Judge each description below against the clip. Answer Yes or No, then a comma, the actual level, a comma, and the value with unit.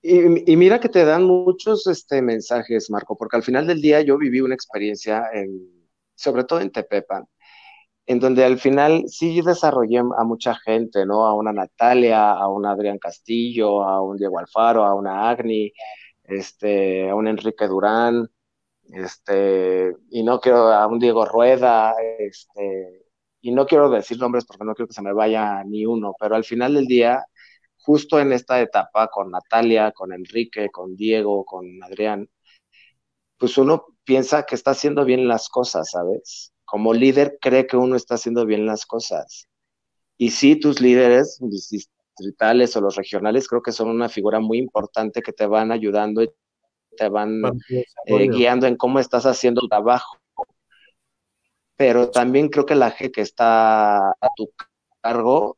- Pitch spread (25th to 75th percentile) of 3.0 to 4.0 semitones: Yes, average, 3.4 semitones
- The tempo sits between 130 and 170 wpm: Yes, average, 165 wpm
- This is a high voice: No, low, 115 Hz